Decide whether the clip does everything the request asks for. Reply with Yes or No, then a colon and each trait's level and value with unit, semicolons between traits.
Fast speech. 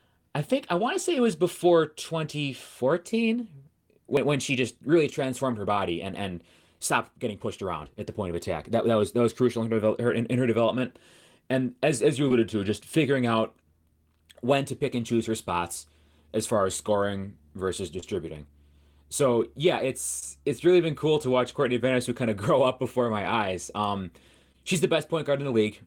Yes: fast, 210 wpm